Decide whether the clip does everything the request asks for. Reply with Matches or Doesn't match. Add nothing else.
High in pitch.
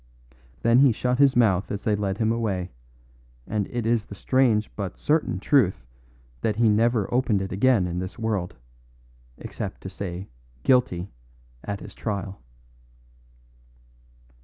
Doesn't match